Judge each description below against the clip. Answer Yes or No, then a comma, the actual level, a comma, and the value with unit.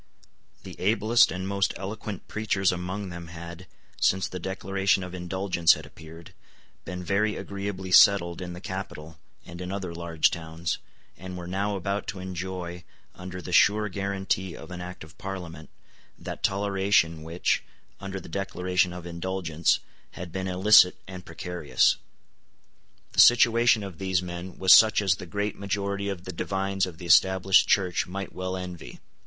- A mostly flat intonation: Yes, narrow, 2.0 semitones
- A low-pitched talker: Yes, very low, 95 Hz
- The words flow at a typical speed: Yes, average, 160 wpm